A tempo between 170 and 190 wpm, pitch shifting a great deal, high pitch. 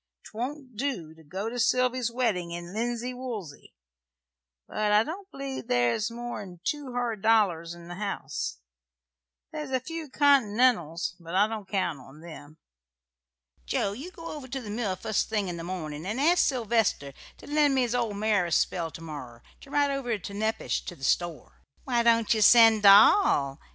Yes: average, 175 wpm; wide, 6.5 semitones; high, 220 Hz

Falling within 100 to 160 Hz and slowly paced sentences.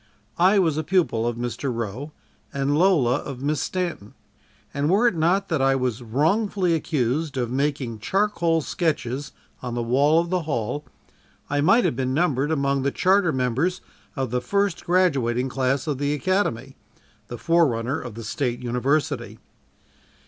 No: medium, 140 Hz; average, 160 wpm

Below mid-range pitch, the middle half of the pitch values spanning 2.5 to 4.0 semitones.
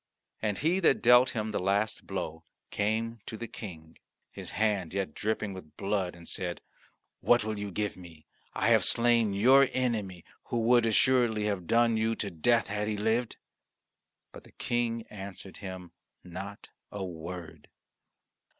Yes: low, 105 Hz; average, 3.7 semitones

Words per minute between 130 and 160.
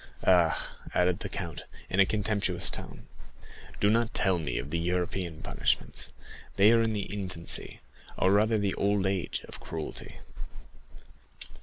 Yes: average, 140 wpm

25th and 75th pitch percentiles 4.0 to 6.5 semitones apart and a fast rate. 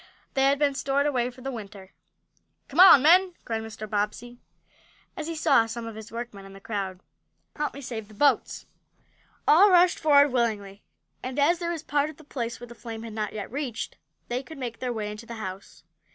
Yes: average, 4.7 semitones; fast, 210 wpm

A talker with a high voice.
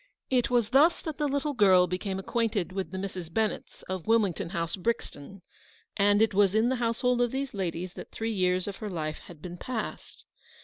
Yes: high, 205 Hz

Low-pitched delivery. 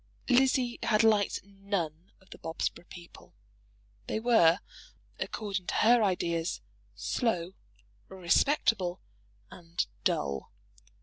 No: high, 190 Hz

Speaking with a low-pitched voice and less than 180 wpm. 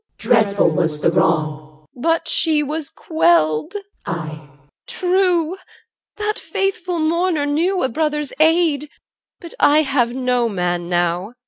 No: very high, 285 Hz; average, 150 wpm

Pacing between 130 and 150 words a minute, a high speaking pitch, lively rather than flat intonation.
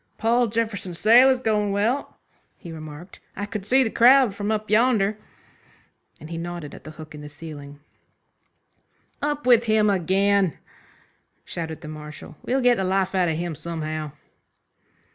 No: average, 160 wpm; high, 195 Hz; wide, 5.7 semitones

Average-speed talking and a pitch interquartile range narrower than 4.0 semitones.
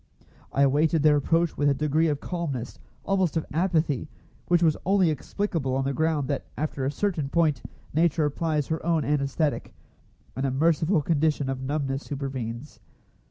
Yes: average, 160 wpm; average, 3.0 semitones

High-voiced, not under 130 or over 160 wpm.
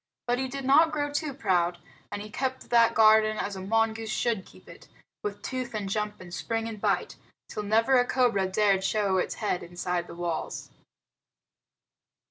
No: high, 215 Hz; average, 180 wpm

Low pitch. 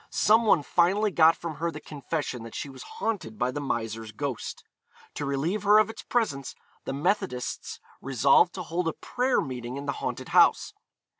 No: medium, 150 Hz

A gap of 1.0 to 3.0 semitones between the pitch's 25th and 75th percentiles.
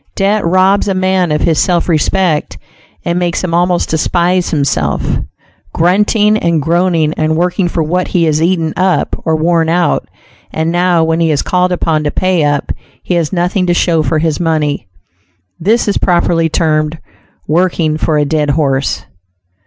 Yes: narrow, 2.5 semitones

